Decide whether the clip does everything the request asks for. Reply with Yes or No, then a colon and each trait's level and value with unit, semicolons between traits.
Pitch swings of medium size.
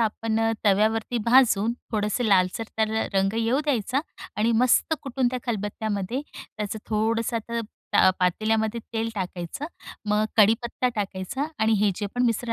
No: narrow, 2.3 semitones